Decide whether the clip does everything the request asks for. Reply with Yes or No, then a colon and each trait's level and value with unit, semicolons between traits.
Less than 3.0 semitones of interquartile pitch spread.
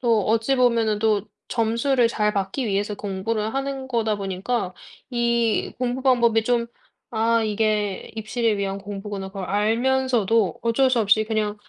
Yes: narrow, 2.5 semitones